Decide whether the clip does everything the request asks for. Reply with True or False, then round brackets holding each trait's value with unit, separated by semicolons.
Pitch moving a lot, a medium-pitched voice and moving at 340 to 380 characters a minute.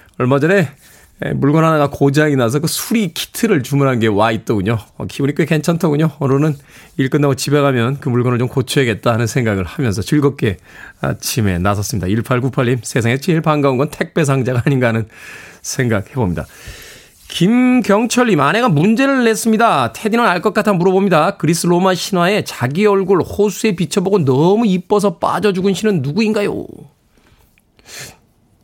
True (7.3 semitones; 150 Hz; 350 characters per minute)